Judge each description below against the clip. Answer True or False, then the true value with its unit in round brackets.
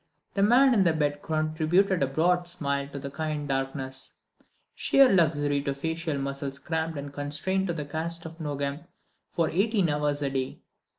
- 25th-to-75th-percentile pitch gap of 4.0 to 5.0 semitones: False (3.3 semitones)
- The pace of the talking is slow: False (160 wpm)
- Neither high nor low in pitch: True (155 Hz)